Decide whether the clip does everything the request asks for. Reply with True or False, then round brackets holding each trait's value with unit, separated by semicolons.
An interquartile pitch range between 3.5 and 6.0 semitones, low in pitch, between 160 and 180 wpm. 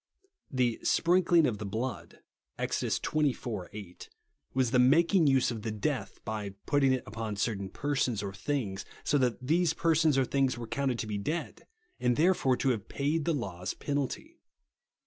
True (5.2 semitones; 130 Hz; 170 wpm)